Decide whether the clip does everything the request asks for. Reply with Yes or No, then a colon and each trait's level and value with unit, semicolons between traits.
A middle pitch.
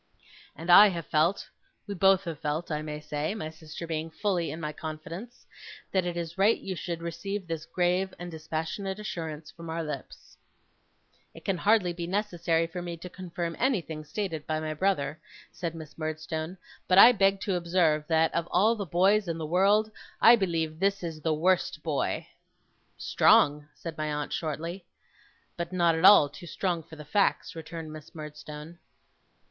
Yes: medium, 170 Hz